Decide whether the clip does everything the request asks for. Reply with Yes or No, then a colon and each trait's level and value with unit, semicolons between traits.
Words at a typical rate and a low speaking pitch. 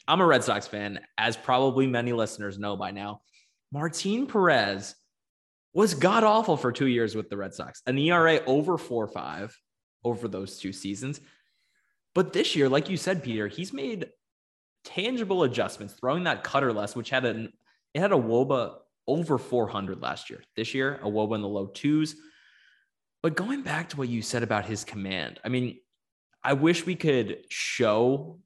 Yes: average, 180 wpm; low, 125 Hz